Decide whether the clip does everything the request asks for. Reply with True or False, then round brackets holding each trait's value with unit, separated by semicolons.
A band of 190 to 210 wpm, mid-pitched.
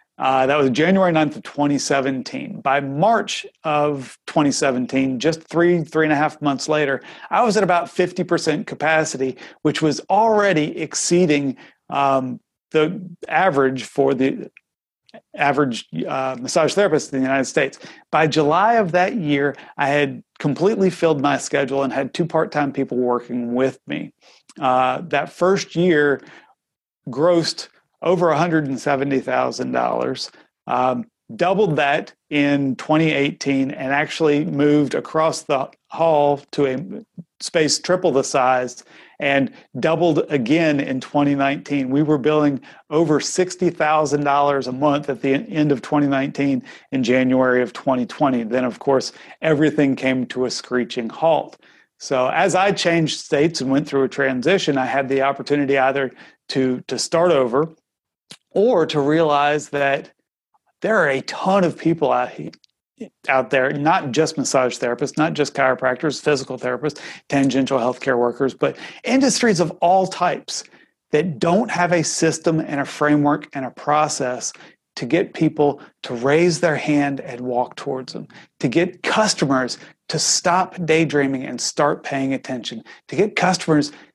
False (145 wpm; 145 Hz)